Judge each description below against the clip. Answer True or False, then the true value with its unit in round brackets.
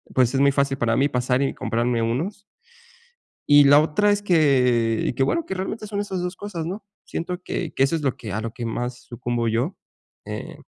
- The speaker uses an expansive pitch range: True (6.7 semitones)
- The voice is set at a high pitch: False (140 Hz)